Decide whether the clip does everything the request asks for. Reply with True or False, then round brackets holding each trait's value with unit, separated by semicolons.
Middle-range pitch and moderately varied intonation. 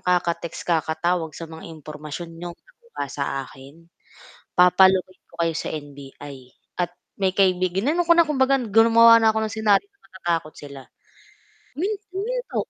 False (180 Hz; 6.0 semitones)